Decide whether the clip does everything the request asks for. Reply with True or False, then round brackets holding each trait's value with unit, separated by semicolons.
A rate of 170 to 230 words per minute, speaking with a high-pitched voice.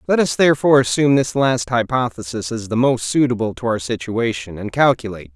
False (180 wpm; 120 Hz)